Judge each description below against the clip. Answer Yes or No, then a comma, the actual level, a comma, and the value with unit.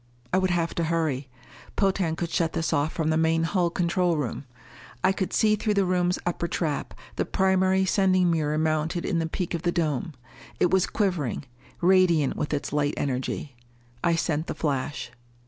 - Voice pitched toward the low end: No, medium, 165 Hz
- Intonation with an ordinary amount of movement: Yes, average, 3.2 semitones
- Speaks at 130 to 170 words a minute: No, average, 180 wpm